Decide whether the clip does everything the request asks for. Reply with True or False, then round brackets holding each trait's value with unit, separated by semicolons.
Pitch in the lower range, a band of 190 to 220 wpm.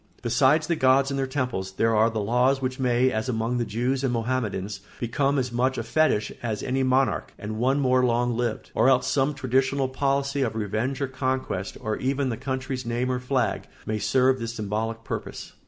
True (125 Hz; 200 wpm)